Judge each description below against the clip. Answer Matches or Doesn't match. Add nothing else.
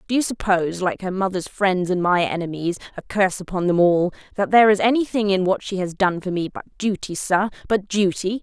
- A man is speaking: Doesn't match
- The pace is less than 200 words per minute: Doesn't match